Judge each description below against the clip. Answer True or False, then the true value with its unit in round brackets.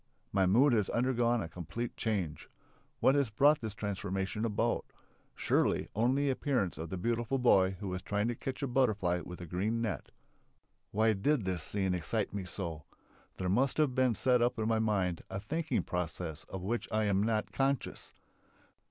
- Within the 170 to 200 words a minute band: True (180 wpm)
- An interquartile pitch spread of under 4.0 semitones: False (4.4 semitones)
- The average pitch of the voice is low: True (110 Hz)